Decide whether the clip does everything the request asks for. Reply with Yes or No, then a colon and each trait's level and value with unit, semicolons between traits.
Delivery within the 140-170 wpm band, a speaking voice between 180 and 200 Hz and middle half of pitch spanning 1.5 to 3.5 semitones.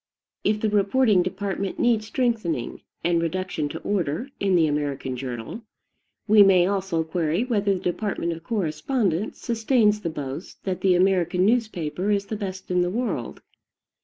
No: average, 155 wpm; high, 190 Hz; average, 4.0 semitones